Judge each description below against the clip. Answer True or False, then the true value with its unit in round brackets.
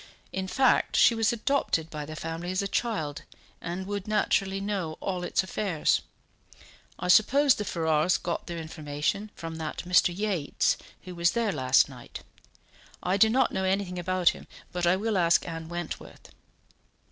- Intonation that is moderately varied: True (3.7 semitones)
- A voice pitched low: False (180 Hz)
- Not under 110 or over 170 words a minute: True (165 wpm)